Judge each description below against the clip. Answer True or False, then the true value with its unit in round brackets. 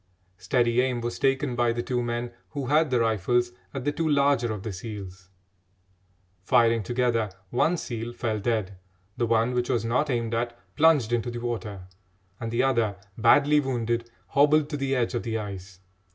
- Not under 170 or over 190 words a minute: True (180 wpm)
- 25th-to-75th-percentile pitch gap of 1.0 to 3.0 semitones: True (2.5 semitones)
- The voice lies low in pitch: True (120 Hz)